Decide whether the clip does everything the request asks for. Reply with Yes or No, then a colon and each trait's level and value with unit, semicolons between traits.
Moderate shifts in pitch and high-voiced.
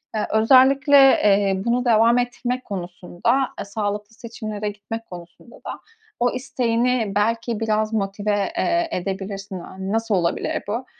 Yes: average, 3.4 semitones; high, 220 Hz